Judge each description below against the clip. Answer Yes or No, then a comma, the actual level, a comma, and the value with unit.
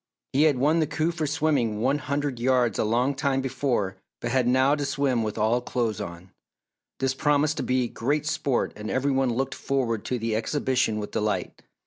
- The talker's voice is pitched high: No, low, 130 Hz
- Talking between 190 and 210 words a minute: Yes, average, 195 wpm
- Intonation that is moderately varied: Yes, average, 3.5 semitones